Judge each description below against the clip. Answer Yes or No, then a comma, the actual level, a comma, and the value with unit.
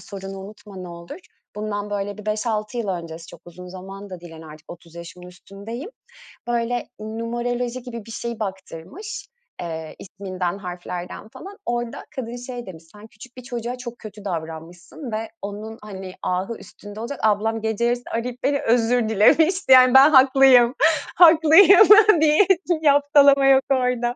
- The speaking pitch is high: Yes, high, 220 Hz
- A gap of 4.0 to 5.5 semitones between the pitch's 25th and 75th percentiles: Yes, average, 4.7 semitones